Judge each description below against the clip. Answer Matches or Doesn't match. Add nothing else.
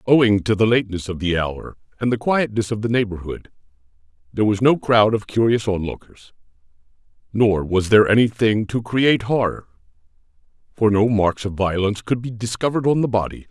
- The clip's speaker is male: Matches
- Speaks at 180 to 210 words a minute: Doesn't match